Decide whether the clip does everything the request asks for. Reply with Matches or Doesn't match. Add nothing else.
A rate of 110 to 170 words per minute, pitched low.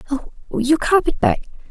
Doesn't match